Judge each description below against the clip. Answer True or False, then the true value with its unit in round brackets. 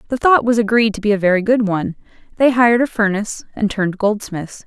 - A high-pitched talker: True (215 Hz)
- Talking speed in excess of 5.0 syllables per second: True (6.3 syllables/s)